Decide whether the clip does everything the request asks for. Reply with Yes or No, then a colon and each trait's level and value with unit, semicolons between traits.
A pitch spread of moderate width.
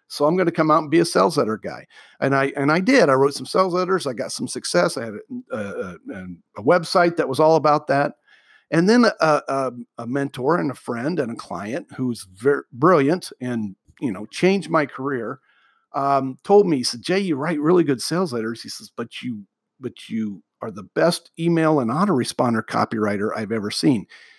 No: wide, 5.8 semitones